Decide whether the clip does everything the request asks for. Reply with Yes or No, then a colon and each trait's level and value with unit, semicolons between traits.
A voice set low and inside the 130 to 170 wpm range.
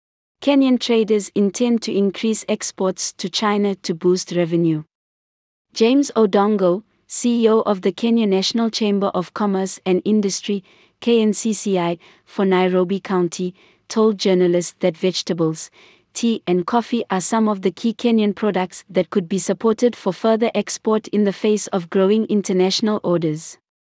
No: high, 200 Hz; average, 140 wpm